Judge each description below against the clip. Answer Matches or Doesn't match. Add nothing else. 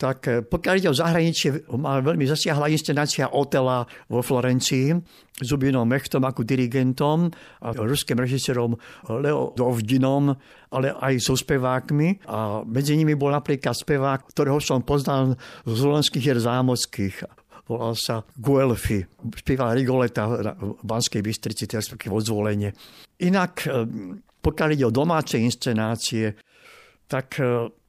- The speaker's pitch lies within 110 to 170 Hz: Matches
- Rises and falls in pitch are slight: Doesn't match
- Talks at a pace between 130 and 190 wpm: Doesn't match